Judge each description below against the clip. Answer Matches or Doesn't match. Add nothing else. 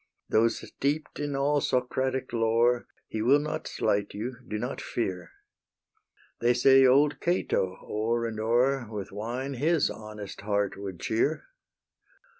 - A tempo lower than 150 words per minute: Matches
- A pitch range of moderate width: Matches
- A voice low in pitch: Matches